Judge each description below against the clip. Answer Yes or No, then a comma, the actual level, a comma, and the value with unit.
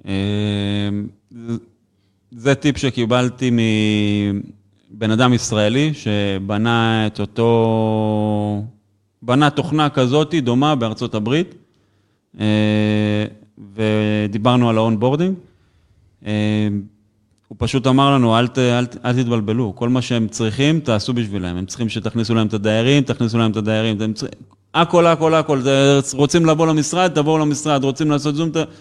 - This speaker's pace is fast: No, average, 125 wpm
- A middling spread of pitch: Yes, average, 4.4 semitones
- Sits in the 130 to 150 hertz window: No, low, 115 Hz